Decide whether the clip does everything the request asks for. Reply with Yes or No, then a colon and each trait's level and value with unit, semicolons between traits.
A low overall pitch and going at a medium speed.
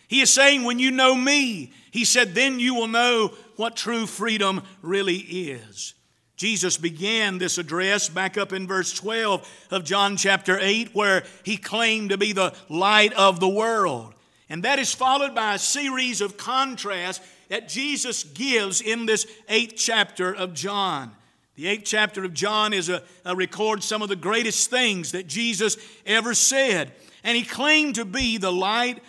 No: high, 210 Hz; average, 175 wpm